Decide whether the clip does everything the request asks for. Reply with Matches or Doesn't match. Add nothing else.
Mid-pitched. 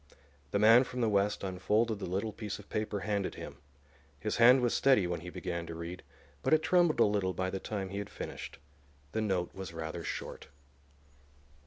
Doesn't match